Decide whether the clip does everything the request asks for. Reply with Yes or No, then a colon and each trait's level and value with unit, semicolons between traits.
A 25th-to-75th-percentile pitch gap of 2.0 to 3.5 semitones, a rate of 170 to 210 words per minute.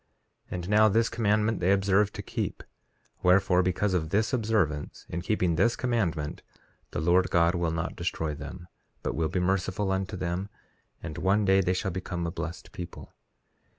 Yes: average, 3.0 semitones; average, 175 wpm